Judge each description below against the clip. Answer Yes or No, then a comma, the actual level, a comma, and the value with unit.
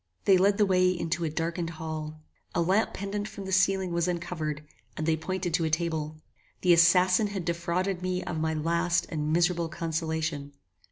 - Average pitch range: No, narrow, 2.3 semitones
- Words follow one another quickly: No, average, 180 wpm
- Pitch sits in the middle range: Yes, medium, 170 Hz